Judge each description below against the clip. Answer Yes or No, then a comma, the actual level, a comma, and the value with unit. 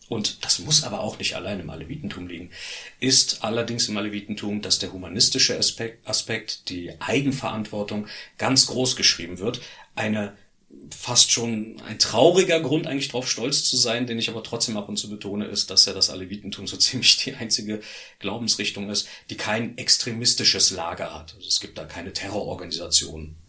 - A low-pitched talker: Yes, low, 105 Hz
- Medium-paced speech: Yes, average, 170 wpm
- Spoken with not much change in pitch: No, average, 3.5 semitones